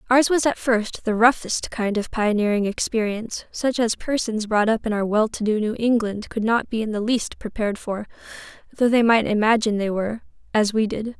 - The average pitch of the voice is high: Yes, high, 220 Hz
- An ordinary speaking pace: No, fast, 210 wpm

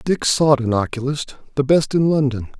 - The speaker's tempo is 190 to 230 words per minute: No, average, 160 wpm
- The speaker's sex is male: Yes, male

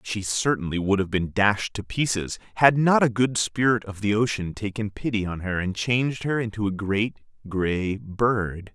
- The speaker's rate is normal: Yes, average, 190 wpm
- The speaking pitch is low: Yes, low, 105 Hz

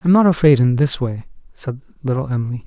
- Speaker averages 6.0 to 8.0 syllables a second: No, 5.7 syllables/s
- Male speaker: Yes, male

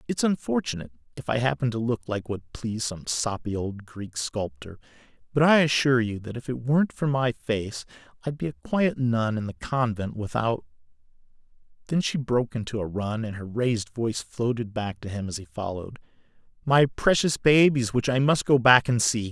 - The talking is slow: No, average, 185 wpm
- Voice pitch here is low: Yes, low, 120 Hz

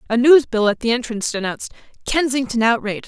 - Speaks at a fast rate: No, average, 175 wpm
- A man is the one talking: No, female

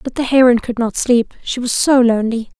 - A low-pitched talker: No, high, 240 Hz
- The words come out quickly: Yes, fast, 230 wpm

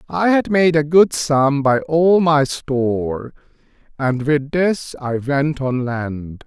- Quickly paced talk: No, average, 160 wpm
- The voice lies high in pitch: No, medium, 145 Hz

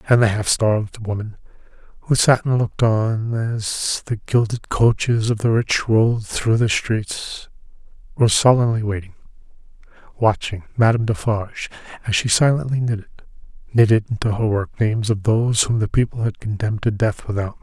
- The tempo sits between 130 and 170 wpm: Yes, average, 155 wpm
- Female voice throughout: No, male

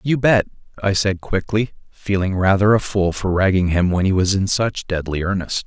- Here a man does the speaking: Yes, male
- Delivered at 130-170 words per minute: No, average, 200 wpm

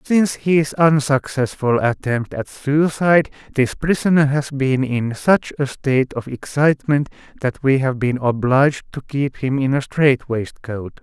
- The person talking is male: Yes, male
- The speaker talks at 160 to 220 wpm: No, average, 150 wpm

